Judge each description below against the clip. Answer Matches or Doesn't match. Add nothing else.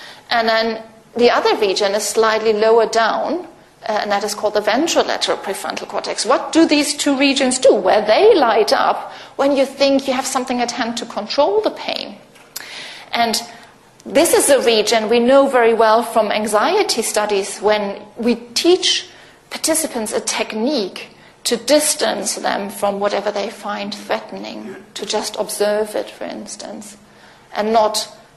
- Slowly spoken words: Doesn't match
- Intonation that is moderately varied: Matches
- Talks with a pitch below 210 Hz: Doesn't match